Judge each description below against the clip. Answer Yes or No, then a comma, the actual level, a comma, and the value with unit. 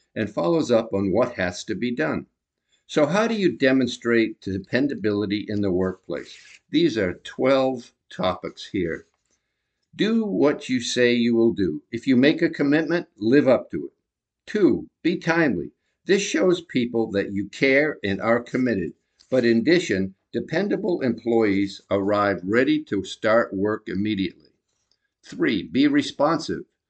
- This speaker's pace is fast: No, average, 145 wpm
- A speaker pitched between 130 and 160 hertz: No, low, 120 Hz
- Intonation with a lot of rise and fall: Yes, wide, 8.2 semitones